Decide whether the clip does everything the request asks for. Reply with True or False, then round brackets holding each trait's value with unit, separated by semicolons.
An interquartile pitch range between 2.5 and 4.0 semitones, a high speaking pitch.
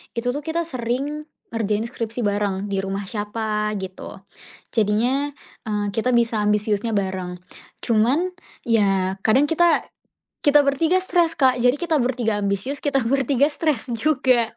False (5.1 semitones; 230 Hz)